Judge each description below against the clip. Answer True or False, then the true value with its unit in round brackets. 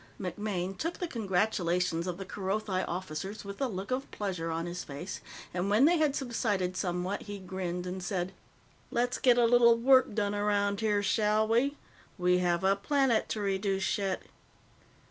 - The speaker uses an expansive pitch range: False (3.7 semitones)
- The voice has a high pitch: True (200 Hz)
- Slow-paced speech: False (170 wpm)